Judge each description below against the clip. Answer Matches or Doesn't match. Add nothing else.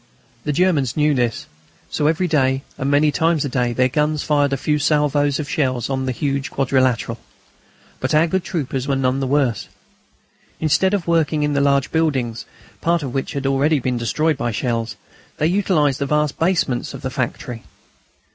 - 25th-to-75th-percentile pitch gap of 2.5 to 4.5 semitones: Matches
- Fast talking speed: Doesn't match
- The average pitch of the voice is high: Doesn't match